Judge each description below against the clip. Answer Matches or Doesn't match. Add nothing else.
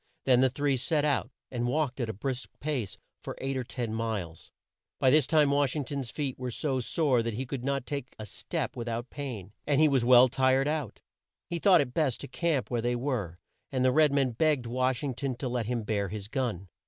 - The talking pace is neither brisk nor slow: Doesn't match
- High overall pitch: Doesn't match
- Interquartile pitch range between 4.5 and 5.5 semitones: Doesn't match